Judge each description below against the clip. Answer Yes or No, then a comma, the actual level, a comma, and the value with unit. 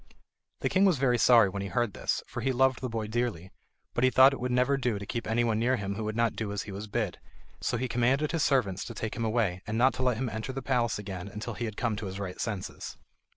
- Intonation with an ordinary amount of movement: Yes, average, 3.5 semitones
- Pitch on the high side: No, low, 115 Hz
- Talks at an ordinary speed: No, fast, 275 wpm